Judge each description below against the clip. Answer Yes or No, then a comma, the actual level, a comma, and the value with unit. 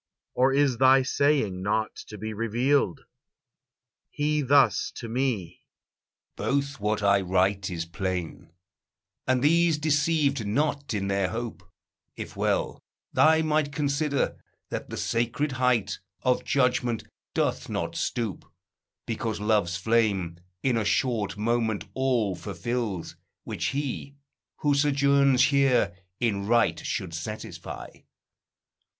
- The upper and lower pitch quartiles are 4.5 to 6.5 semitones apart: Yes, average, 5.3 semitones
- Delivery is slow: Yes, slow, 120 wpm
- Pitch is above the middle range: No, low, 120 Hz